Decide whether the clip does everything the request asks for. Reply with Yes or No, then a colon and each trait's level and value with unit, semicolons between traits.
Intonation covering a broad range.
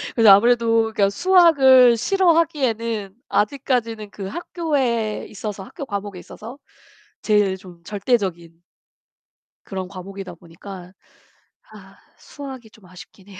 No: average, 4.8 semitones